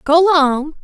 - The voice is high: Yes, very high, 310 Hz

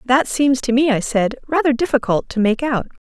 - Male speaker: No, female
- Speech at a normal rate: No, fast, 215 wpm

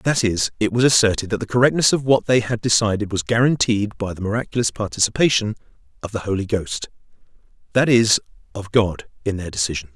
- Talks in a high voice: No, low, 110 Hz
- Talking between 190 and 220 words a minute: No, average, 180 wpm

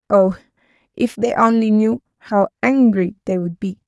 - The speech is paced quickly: No, average, 155 wpm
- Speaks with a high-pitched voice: Yes, high, 210 Hz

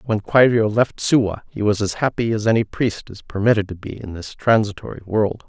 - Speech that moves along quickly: Yes, fast, 210 wpm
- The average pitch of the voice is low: Yes, low, 105 Hz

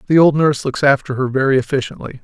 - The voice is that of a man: Yes, male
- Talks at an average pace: No, fast, 215 wpm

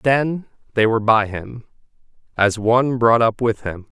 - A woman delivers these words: No, male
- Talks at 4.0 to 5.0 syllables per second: Yes, 4.4 syllables/s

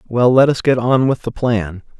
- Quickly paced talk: Yes, fast, 240 wpm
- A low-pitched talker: Yes, low, 120 Hz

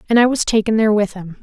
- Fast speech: Yes, fast, 295 wpm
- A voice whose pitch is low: No, high, 215 Hz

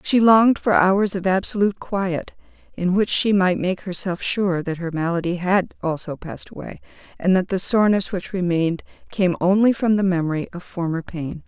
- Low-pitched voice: No, medium, 185 Hz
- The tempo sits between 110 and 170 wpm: No, average, 185 wpm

